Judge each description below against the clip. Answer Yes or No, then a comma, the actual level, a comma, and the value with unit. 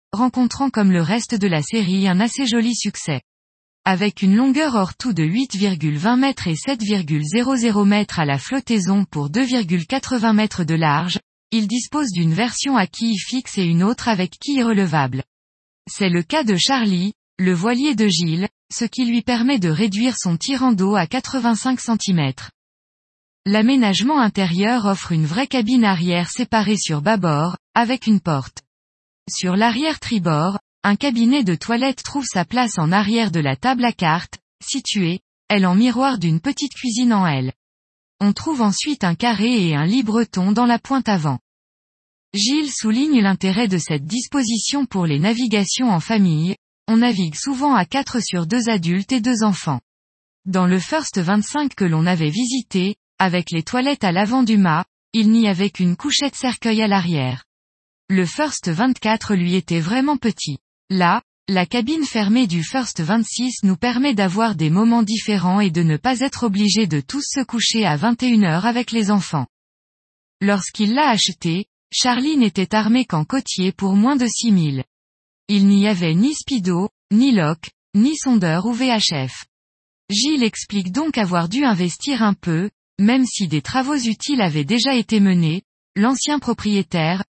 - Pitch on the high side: Yes, high, 210 Hz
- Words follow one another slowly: No, average, 160 wpm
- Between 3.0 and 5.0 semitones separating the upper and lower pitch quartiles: No, wide, 5.6 semitones